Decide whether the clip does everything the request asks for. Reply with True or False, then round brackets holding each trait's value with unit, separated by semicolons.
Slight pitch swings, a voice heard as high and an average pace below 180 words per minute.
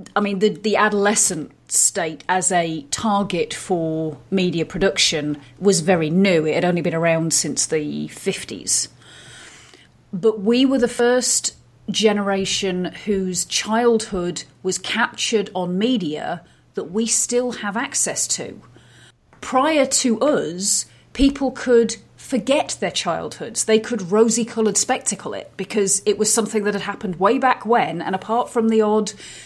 False (4.1 semitones; 205 Hz; 145 wpm)